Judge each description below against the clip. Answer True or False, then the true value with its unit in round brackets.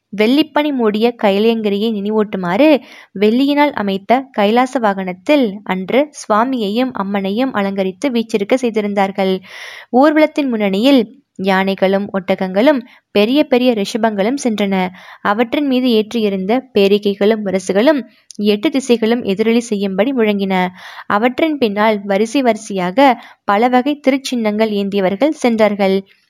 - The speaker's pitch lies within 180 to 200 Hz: False (220 Hz)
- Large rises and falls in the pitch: False (4.3 semitones)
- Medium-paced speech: True (95 wpm)